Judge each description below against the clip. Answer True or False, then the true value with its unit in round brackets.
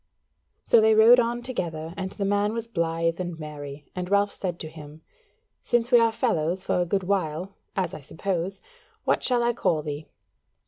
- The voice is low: False (185 Hz)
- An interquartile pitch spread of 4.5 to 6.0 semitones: True (5.4 semitones)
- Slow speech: False (185 wpm)